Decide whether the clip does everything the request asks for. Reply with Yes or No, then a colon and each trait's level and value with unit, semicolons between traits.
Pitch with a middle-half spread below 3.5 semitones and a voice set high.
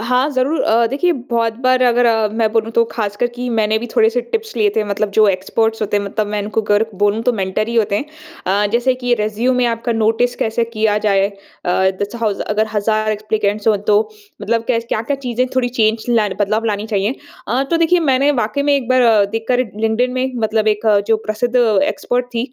Yes: narrow, 2.5 semitones; high, 225 Hz